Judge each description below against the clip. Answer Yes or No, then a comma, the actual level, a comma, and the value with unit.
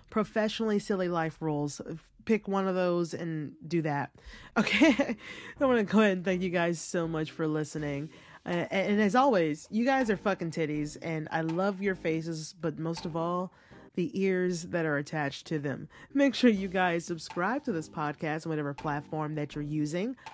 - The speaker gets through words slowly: No, average, 190 wpm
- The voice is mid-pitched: Yes, medium, 170 Hz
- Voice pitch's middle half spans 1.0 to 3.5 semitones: No, average, 4.2 semitones